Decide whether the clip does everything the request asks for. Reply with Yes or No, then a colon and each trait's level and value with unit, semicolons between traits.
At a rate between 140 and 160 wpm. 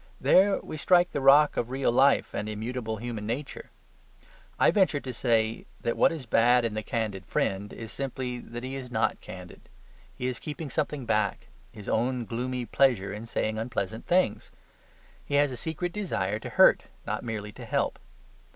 No: average, 180 wpm